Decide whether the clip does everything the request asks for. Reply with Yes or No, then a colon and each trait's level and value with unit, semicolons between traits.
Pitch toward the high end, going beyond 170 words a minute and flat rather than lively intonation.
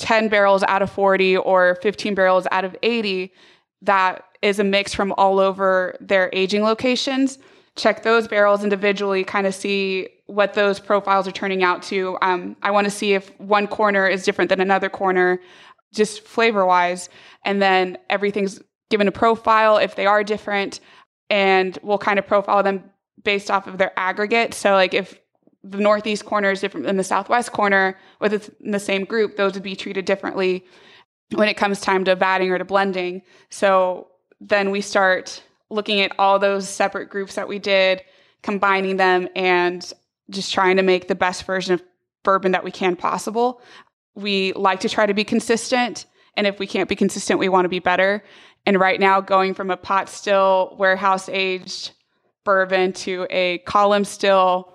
Yes: high, 195 Hz; average, 185 wpm; narrow, 1.5 semitones